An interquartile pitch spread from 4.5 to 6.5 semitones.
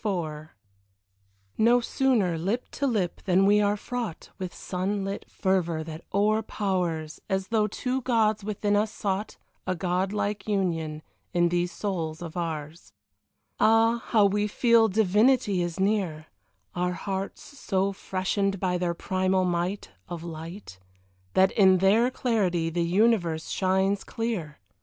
No: average, 3.4 semitones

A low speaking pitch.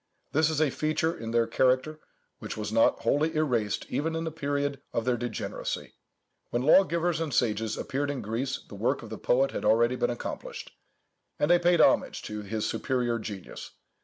Yes: low, 130 Hz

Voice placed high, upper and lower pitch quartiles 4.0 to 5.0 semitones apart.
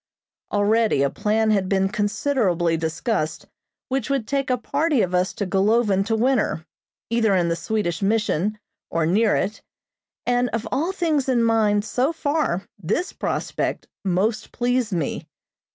Yes: high, 215 Hz; average, 4.5 semitones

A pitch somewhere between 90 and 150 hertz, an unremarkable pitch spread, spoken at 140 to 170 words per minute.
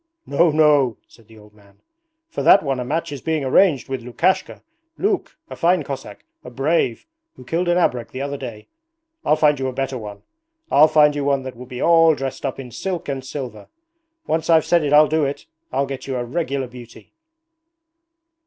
No: medium, 140 Hz; average, 3.7 semitones; average, 200 wpm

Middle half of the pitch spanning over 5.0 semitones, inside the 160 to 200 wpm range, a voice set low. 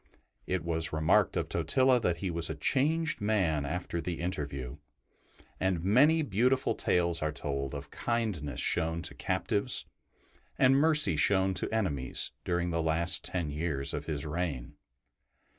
No: wide, 5.4 semitones; average, 145 wpm; very low, 85 Hz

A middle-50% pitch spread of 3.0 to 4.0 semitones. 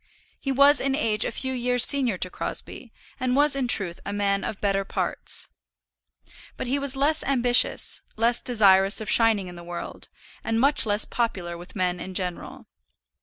No: average, 5.2 semitones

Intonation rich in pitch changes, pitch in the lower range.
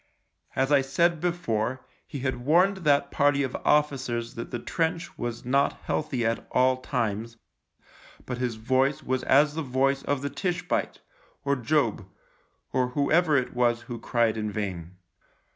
No: average, 3.7 semitones; low, 130 Hz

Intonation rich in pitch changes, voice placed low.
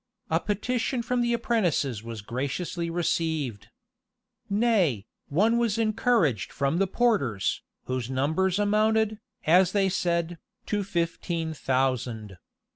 No: wide, 8.1 semitones; medium, 175 Hz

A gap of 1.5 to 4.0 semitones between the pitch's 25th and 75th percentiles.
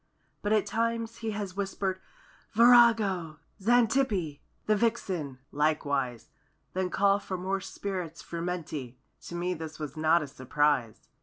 No: average, 5.3 semitones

